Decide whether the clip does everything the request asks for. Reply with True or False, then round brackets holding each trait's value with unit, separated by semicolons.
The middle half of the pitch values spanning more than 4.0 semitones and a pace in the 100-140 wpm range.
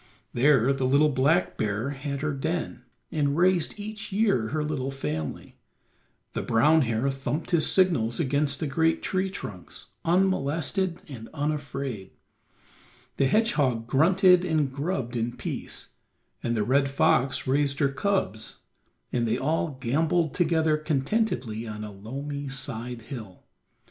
True (4.6 semitones; 135 wpm)